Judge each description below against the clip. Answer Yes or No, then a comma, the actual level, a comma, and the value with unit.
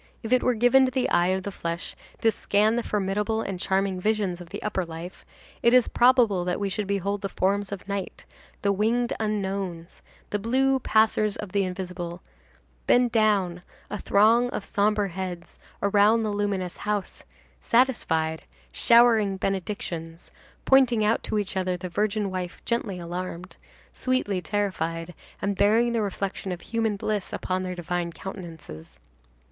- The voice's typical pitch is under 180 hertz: No, high, 200 Hz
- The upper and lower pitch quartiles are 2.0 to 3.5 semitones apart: Yes, average, 3.1 semitones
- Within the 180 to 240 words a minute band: No, average, 160 wpm